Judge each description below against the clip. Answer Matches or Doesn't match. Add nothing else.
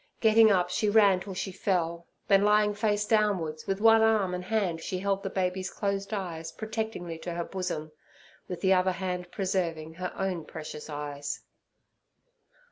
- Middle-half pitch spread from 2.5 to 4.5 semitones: Matches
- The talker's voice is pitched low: Doesn't match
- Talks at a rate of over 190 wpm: Doesn't match